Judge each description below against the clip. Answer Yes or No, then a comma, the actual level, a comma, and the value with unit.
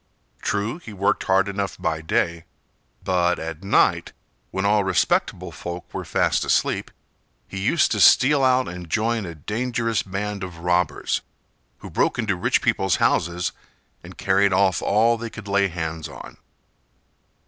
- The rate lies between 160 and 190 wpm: No, average, 150 wpm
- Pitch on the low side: Yes, very low, 95 Hz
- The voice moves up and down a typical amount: Yes, average, 3.5 semitones